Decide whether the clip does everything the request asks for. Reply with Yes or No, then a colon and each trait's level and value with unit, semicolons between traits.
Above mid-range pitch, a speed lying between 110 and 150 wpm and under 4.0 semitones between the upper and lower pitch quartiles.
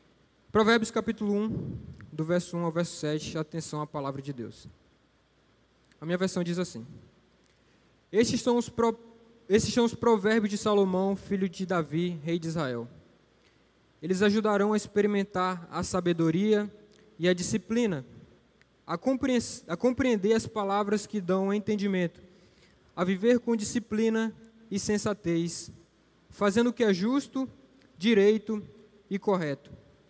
No: high, 200 Hz; average, 135 wpm; average, 4.3 semitones